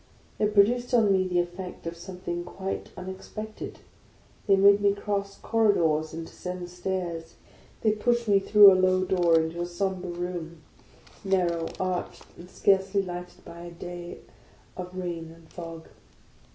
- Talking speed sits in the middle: Yes, average, 150 wpm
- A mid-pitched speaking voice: Yes, medium, 180 Hz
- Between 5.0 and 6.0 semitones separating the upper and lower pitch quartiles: No, narrow, 2.4 semitones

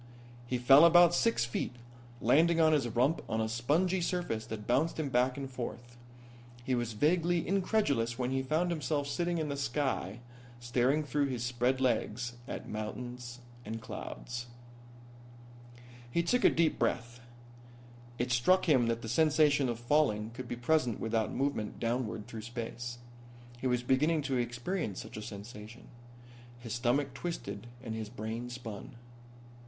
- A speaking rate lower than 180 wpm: Yes, average, 155 wpm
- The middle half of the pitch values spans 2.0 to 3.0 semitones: No, average, 4.2 semitones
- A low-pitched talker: Yes, low, 125 Hz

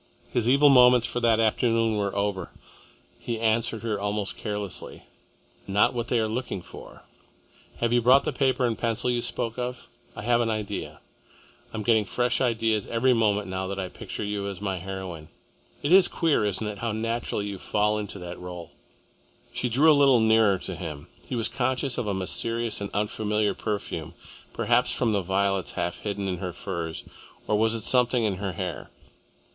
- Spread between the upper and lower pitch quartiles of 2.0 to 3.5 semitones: Yes, average, 3.2 semitones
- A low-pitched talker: Yes, low, 110 Hz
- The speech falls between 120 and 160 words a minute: No, average, 185 wpm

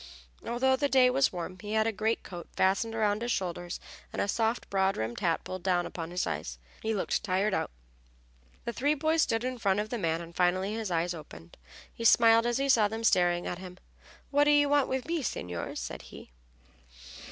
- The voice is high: Yes, high, 210 Hz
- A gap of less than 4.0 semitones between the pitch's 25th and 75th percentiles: No, average, 5.1 semitones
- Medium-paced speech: No, fast, 210 wpm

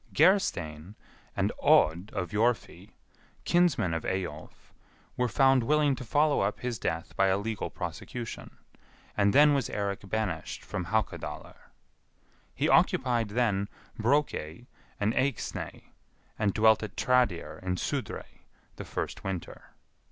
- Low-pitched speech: Yes, low, 110 Hz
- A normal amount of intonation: Yes, average, 4.9 semitones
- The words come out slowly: Yes, slow, 125 wpm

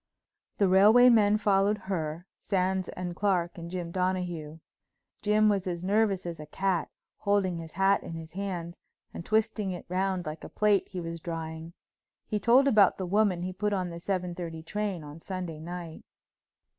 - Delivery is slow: No, average, 175 wpm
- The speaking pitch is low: No, medium, 185 Hz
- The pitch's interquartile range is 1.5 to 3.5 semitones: Yes, average, 3.0 semitones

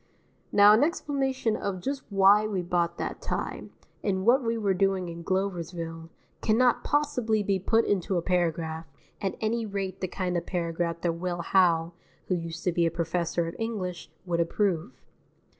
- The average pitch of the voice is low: No, medium, 185 Hz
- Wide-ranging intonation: No, average, 3.8 semitones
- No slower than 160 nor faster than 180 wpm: Yes, average, 170 wpm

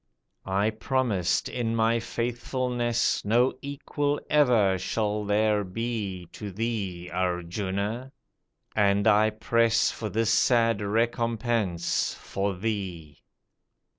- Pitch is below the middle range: Yes, low, 110 Hz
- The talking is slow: Yes, slow, 100 wpm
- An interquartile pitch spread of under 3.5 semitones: Yes, average, 2.9 semitones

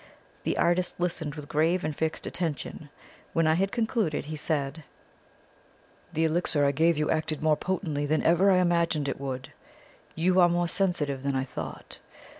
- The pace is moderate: Yes, average, 170 wpm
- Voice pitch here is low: No, medium, 160 Hz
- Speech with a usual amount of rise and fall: Yes, average, 3.0 semitones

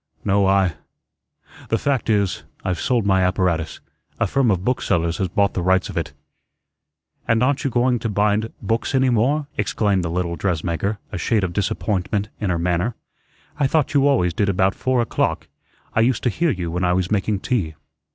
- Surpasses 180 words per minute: Yes, average, 190 wpm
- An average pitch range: Yes, average, 4.5 semitones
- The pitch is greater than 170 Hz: No, low, 100 Hz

